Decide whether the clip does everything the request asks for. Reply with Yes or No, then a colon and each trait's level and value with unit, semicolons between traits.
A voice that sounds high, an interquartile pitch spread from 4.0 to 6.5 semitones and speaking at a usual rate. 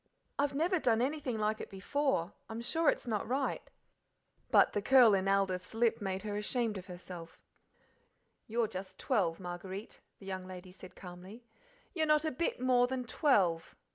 Yes: high, 215 Hz; average, 5.3 semitones; average, 170 wpm